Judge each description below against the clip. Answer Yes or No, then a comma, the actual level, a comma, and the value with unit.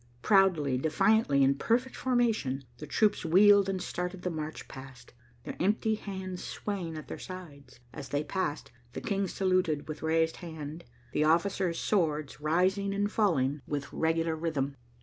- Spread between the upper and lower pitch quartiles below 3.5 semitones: No, average, 4.6 semitones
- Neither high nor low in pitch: Yes, medium, 165 Hz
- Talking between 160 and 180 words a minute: No, average, 150 wpm